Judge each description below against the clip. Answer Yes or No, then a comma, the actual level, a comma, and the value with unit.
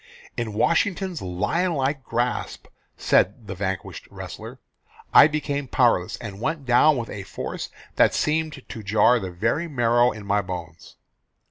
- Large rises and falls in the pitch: Yes, wide, 6.5 semitones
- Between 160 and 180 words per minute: No, average, 145 wpm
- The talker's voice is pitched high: No, low, 120 Hz